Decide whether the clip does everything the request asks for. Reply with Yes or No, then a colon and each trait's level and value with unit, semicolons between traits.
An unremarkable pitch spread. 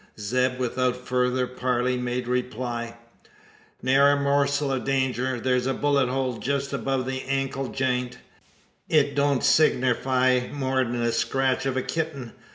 No: narrow, 1.4 semitones